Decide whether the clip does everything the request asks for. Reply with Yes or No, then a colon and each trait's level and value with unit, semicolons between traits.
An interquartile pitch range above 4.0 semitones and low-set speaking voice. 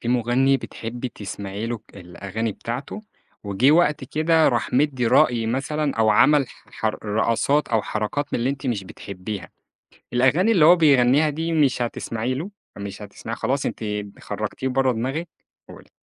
Yes: average, 4.5 semitones; low, 125 Hz